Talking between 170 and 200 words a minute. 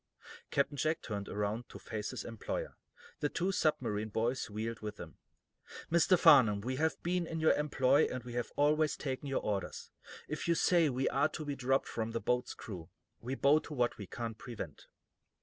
Yes: average, 195 wpm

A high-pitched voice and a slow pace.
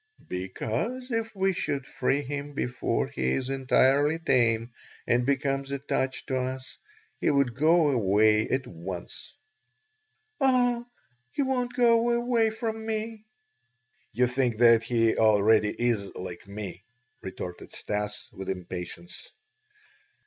No: low, 130 Hz; slow, 120 wpm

